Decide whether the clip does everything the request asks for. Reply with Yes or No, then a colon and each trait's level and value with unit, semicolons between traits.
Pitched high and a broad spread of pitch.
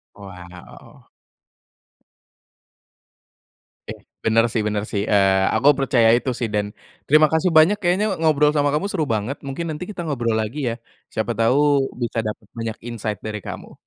No: low, 120 Hz; wide, 6.1 semitones